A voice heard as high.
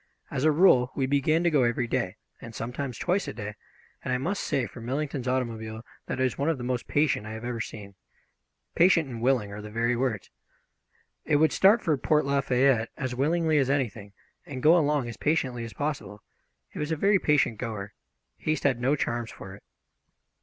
No: low, 130 Hz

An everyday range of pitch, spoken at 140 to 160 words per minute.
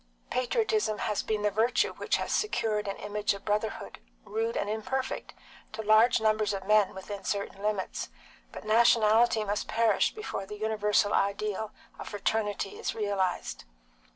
No: narrow, 1.4 semitones; average, 150 wpm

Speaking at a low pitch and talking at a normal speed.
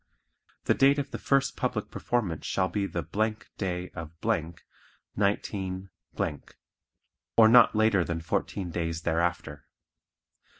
No: very low, 95 Hz; slow, 115 wpm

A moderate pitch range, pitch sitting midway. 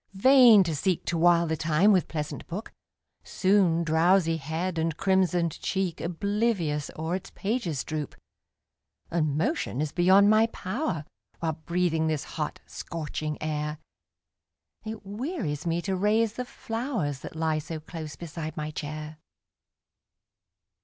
Yes: average, 4.2 semitones; medium, 170 Hz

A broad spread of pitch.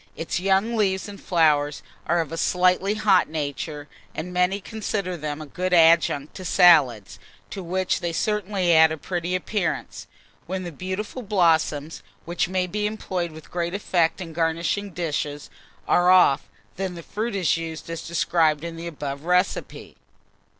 No: average, 2.8 semitones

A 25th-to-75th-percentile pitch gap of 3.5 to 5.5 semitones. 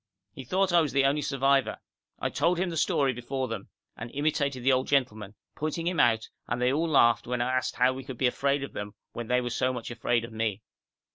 No: average, 2.9 semitones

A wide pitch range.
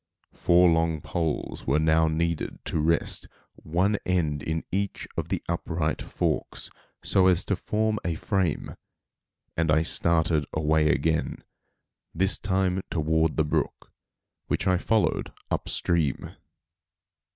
No: narrow, 2.6 semitones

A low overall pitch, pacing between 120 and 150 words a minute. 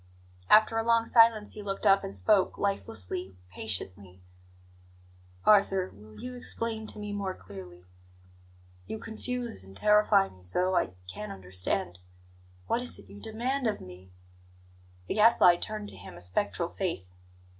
No: high, 190 Hz; average, 145 wpm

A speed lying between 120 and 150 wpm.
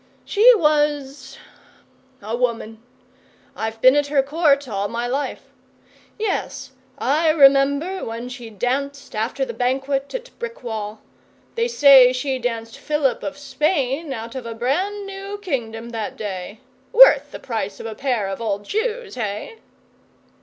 Yes: average, 140 wpm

